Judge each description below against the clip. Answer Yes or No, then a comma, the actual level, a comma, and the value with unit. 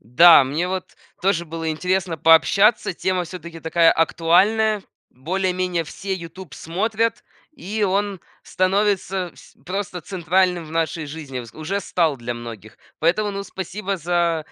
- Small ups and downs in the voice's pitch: No, average, 3.0 semitones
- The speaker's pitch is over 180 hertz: No, medium, 175 Hz